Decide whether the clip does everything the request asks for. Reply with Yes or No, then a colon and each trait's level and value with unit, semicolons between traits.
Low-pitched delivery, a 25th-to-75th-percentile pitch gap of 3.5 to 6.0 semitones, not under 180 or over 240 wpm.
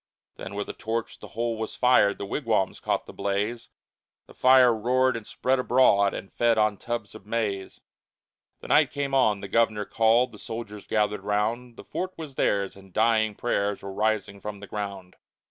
No: low, 110 Hz; average, 2.7 semitones; average, 185 wpm